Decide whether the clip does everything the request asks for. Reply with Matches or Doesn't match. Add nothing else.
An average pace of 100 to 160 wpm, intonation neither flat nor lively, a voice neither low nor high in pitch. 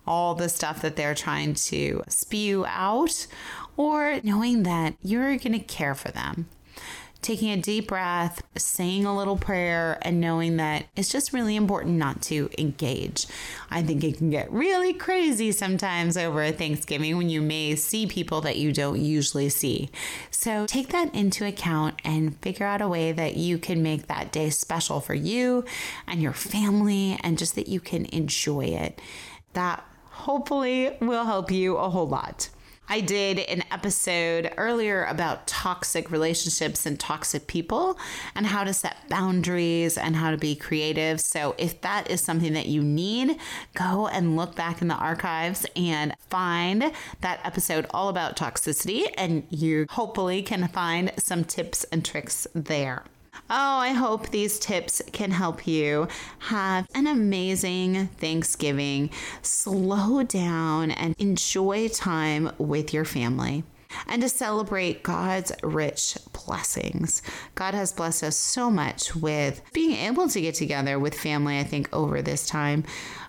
Matches